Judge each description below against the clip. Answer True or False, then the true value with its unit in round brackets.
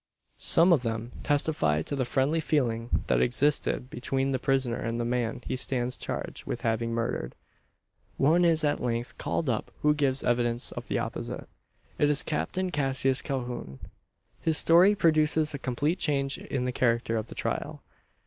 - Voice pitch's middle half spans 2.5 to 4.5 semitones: True (3.9 semitones)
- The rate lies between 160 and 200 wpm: True (170 wpm)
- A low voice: True (130 Hz)